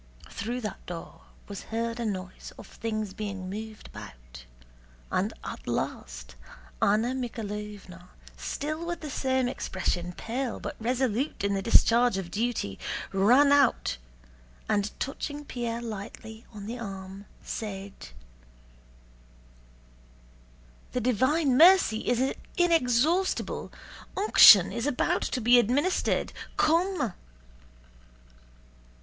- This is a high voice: Yes, high, 230 Hz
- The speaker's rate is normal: No, slow, 110 wpm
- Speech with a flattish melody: No, average, 4.6 semitones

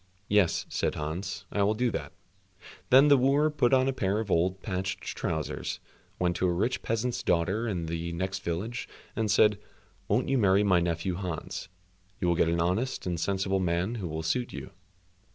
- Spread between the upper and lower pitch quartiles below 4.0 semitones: No, average, 4.3 semitones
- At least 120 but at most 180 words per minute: No, average, 190 wpm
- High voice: No, very low, 95 Hz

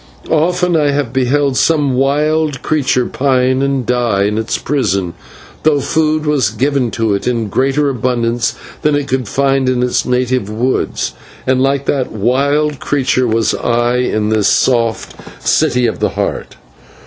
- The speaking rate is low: No, average, 155 wpm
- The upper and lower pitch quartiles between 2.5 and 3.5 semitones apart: Yes, average, 3.0 semitones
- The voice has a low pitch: Yes, low, 130 Hz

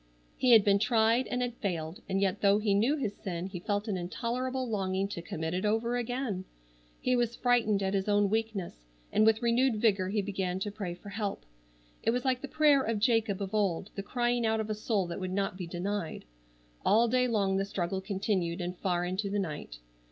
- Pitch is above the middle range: Yes, high, 205 Hz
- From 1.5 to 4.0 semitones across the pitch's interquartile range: Yes, average, 3.5 semitones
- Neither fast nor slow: No, fast, 215 wpm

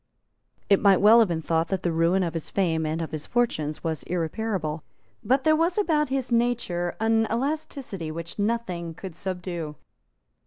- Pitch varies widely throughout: Yes, wide, 6.1 semitones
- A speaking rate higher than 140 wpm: Yes, average, 170 wpm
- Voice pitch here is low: No, medium, 185 Hz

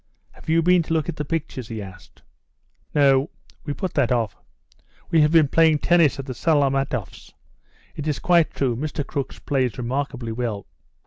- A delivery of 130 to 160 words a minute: No, average, 175 wpm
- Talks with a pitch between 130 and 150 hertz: Yes, medium, 140 Hz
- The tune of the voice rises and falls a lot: No, average, 4.1 semitones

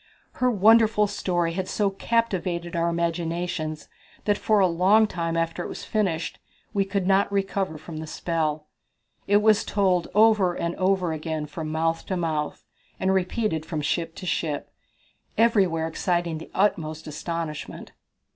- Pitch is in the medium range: Yes, medium, 175 Hz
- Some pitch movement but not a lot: Yes, average, 3.4 semitones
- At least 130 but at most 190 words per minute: Yes, average, 150 wpm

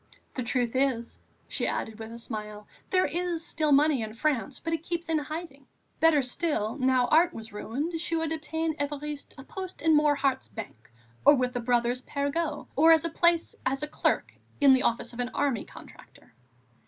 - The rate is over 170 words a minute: Yes, average, 180 wpm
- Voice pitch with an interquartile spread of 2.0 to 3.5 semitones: No, average, 4.7 semitones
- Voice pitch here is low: No, very high, 285 Hz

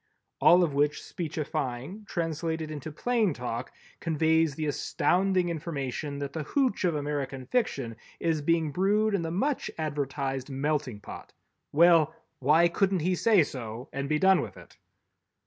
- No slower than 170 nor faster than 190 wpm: No, average, 145 wpm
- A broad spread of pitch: No, average, 3.9 semitones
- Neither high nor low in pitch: Yes, medium, 155 Hz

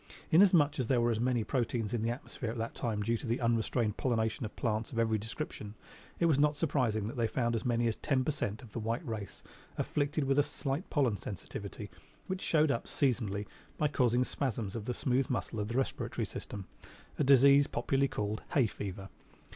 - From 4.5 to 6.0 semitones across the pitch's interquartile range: No, average, 3.8 semitones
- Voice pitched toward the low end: Yes, low, 120 Hz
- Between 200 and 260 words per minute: Yes, fast, 205 wpm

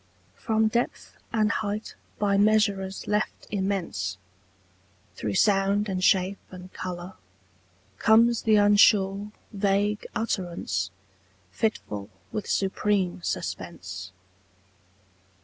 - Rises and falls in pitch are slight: Yes, narrow, 2.2 semitones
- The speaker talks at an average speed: No, slow, 90 wpm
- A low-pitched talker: No, high, 200 Hz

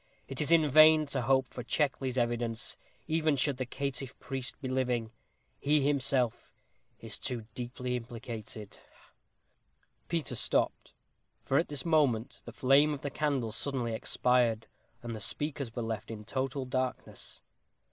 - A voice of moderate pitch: No, low, 130 Hz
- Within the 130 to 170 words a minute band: Yes, average, 145 wpm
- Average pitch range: Yes, average, 3.1 semitones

